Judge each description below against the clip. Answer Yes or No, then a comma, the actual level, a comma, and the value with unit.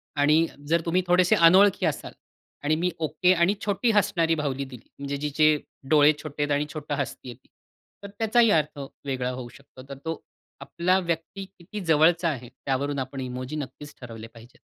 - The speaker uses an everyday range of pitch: Yes, average, 4.0 semitones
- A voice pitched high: No, medium, 150 Hz